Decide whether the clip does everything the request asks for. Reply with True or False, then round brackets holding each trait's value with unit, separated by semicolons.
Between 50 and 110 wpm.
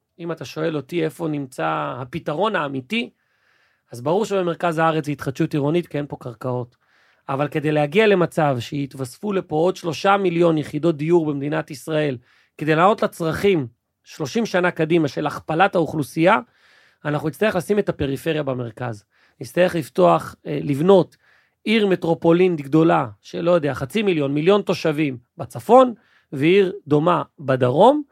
False (135 wpm)